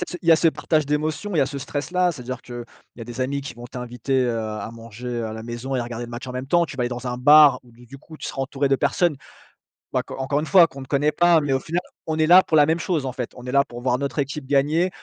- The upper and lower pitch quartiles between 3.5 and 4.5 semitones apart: Yes, average, 3.8 semitones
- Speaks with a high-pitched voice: No, low, 135 Hz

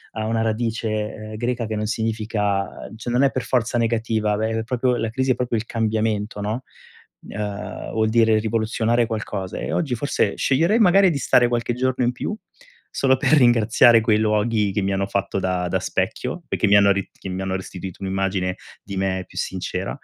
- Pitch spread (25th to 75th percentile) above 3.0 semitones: No, average, 2.7 semitones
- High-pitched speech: No, low, 110 Hz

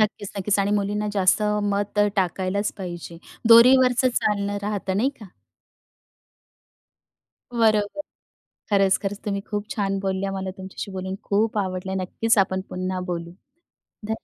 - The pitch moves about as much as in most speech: No, narrow, 1.9 semitones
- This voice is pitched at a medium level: No, high, 200 Hz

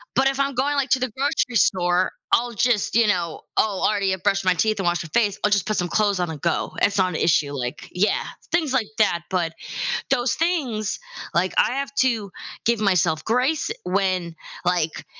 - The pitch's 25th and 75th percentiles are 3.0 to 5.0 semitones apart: No, wide, 5.5 semitones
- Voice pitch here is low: No, high, 205 Hz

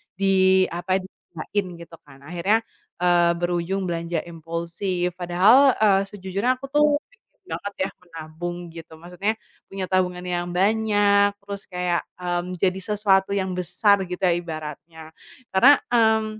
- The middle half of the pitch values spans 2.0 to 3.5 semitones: Yes, narrow, 2.6 semitones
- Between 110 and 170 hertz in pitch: No, medium, 185 Hz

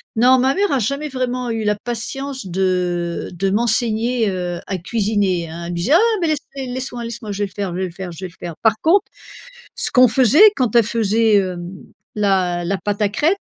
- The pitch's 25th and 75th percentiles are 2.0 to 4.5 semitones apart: No, average, 5.2 semitones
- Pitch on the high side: Yes, high, 220 Hz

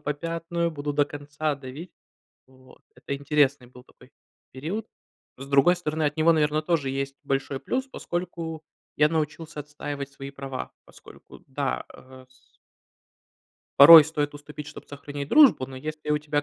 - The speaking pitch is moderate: Yes, medium, 145 Hz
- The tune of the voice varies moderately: No, narrow, 2.3 semitones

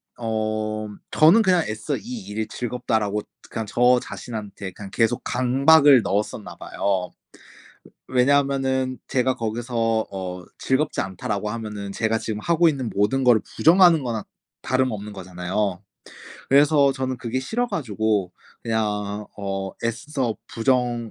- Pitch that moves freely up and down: No, average, 4.0 semitones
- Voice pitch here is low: Yes, low, 115 Hz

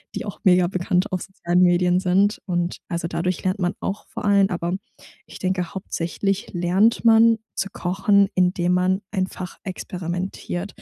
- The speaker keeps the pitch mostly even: Yes, narrow, 1.8 semitones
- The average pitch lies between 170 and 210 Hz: Yes, medium, 185 Hz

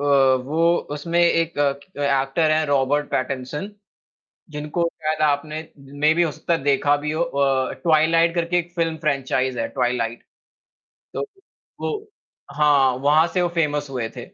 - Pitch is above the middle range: No, medium, 150 Hz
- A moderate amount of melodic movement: Yes, average, 3.2 semitones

